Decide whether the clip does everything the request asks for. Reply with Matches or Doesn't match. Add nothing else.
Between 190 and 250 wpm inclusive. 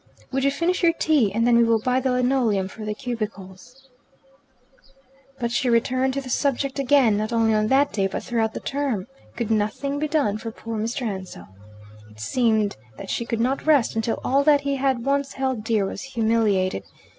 Matches